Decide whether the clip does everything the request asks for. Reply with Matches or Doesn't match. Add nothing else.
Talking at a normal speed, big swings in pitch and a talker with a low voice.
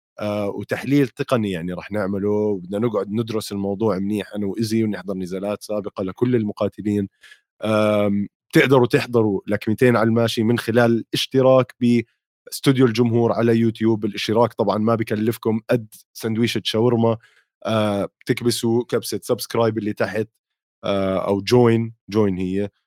Doesn't match